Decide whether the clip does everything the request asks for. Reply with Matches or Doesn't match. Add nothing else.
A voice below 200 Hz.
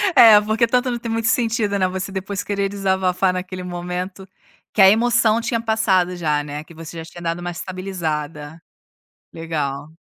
Matches